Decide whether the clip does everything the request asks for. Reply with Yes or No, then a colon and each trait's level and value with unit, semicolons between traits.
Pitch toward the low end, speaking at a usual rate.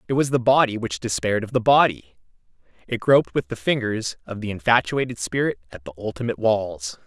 Yes: low, 110 Hz; average, 180 wpm